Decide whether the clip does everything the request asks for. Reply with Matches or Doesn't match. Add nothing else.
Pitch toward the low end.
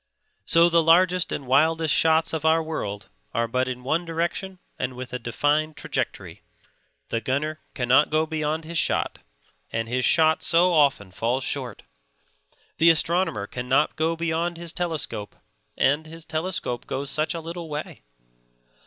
Doesn't match